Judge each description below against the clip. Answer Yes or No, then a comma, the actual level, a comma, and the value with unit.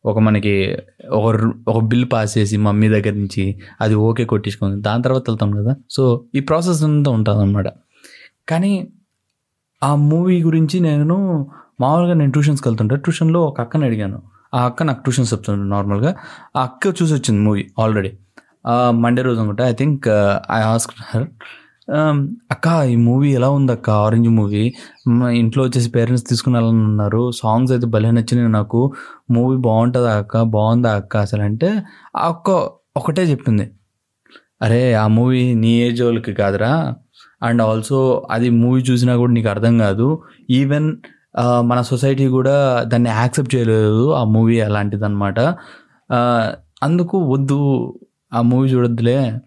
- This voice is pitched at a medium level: No, low, 120 Hz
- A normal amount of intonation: Yes, average, 3.6 semitones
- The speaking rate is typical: No, fast, 140 wpm